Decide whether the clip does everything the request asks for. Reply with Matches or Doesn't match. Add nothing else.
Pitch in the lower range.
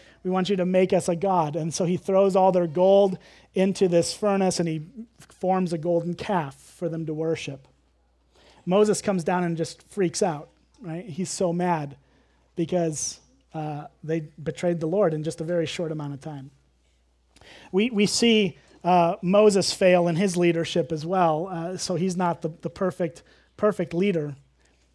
Doesn't match